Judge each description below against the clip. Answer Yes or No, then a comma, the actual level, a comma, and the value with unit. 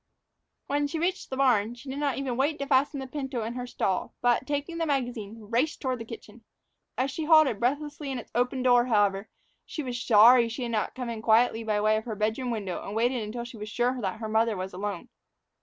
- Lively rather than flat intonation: No, average, 3.5 semitones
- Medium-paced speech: No, fast, 235 wpm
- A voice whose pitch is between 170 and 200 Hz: No, high, 240 Hz